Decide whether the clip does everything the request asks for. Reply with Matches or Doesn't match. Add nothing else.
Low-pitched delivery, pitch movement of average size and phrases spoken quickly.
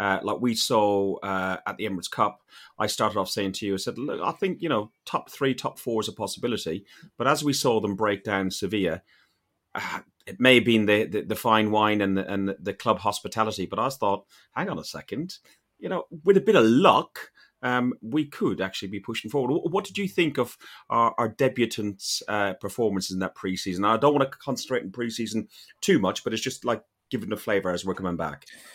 Matches